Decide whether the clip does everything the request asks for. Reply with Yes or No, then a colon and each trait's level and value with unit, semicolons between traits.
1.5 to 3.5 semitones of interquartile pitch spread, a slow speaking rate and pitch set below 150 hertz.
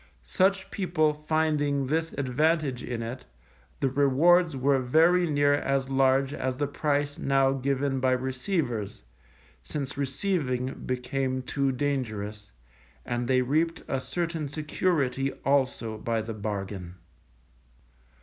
Yes: average, 3.0 semitones; slow, 120 wpm; low, 135 Hz